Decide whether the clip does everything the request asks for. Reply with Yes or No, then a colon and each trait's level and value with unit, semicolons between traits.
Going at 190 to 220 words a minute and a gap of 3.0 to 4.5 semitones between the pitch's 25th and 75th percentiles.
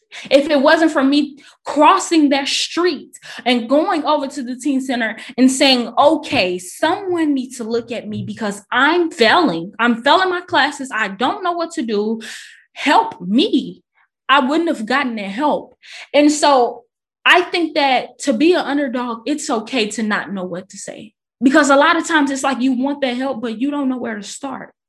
Yes: average, 195 wpm; average, 4.1 semitones